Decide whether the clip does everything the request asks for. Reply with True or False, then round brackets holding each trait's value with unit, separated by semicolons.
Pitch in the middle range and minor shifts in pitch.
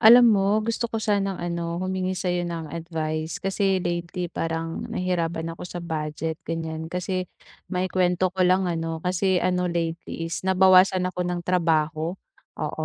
True (180 Hz; 2.1 semitones)